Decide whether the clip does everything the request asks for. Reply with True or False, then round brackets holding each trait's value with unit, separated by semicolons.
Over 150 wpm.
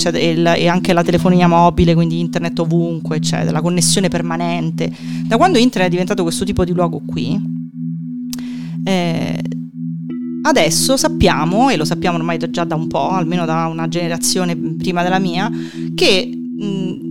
False (145 wpm)